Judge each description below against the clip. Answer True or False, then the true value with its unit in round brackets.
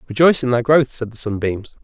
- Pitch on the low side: True (125 Hz)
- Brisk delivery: True (230 wpm)